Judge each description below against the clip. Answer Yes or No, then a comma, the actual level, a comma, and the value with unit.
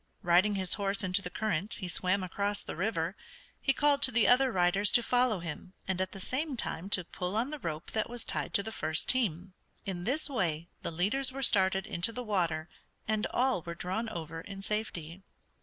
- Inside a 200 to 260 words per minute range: Yes, fast, 205 wpm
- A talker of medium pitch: No, high, 195 Hz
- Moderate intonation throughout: Yes, average, 4.4 semitones